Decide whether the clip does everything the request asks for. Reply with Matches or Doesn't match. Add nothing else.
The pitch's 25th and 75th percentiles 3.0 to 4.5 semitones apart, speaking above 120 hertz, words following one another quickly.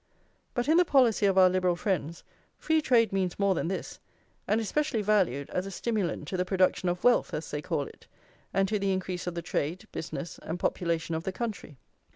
Matches